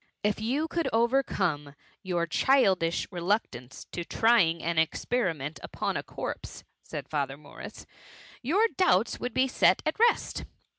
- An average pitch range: No, wide, 7.6 semitones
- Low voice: No, high, 190 Hz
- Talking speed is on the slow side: No, average, 145 wpm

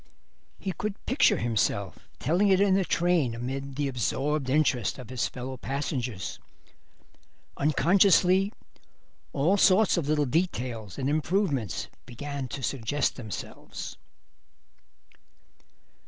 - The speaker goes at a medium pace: No, slow, 110 wpm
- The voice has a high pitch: No, medium, 140 Hz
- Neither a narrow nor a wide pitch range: No, wide, 6.1 semitones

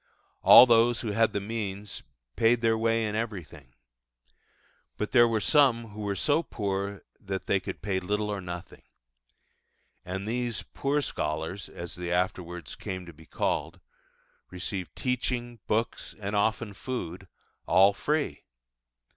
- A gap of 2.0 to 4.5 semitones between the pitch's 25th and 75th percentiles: Yes, average, 3.6 semitones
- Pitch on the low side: Yes, low, 105 Hz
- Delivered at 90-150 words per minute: Yes, average, 140 wpm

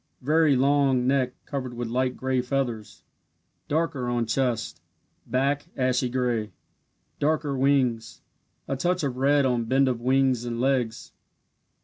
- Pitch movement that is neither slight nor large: No, narrow, 2.1 semitones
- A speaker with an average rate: No, slow, 130 wpm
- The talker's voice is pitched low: Yes, low, 130 Hz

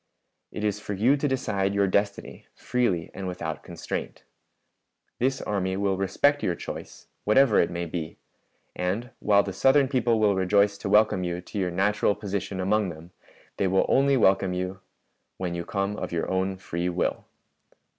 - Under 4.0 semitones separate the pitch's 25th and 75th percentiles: Yes, narrow, 2.6 semitones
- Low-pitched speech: Yes, low, 100 Hz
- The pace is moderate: Yes, average, 170 wpm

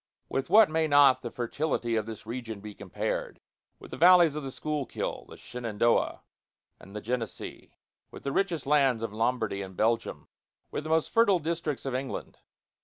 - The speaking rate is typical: Yes, average, 175 wpm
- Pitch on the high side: No, low, 130 Hz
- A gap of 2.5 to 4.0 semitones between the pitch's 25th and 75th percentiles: No, wide, 5.5 semitones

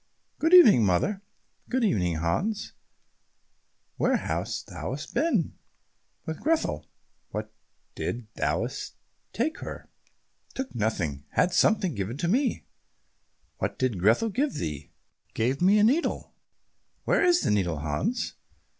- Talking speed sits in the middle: No, slow, 120 wpm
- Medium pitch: Yes, medium, 160 Hz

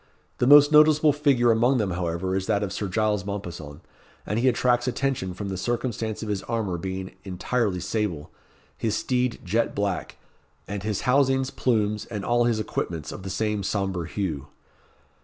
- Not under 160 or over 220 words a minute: Yes, average, 170 wpm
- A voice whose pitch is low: Yes, low, 105 Hz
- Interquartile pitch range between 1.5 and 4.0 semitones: No, average, 4.4 semitones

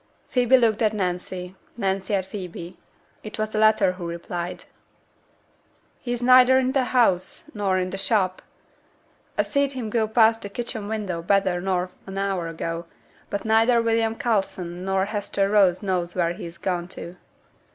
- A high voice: Yes, high, 195 Hz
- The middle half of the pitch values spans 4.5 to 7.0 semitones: No, average, 3.6 semitones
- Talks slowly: No, average, 160 wpm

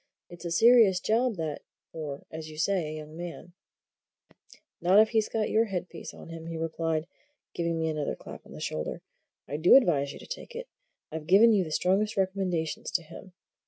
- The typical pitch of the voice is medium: Yes, medium, 170 Hz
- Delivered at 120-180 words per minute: No, average, 195 wpm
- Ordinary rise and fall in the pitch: Yes, average, 4.0 semitones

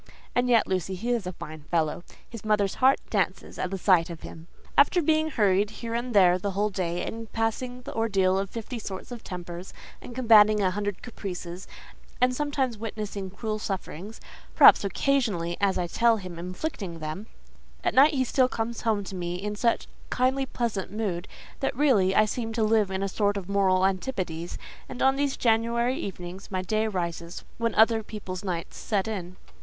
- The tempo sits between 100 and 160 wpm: No, average, 180 wpm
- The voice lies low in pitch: No, high, 205 Hz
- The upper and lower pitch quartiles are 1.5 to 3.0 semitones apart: No, average, 4.0 semitones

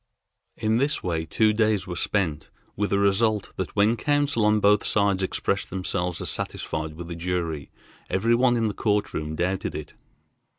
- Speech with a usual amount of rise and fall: Yes, average, 3.6 semitones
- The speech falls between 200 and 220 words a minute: No, average, 175 wpm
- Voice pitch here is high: No, low, 100 Hz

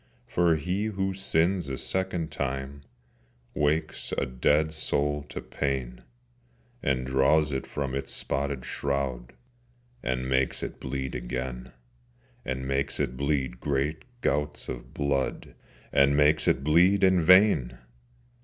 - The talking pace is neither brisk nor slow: No, slow, 125 wpm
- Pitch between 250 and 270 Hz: No, very low, 70 Hz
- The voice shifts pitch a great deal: No, average, 3.2 semitones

